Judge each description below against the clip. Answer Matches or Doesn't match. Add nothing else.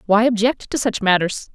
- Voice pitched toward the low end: Doesn't match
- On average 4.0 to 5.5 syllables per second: Matches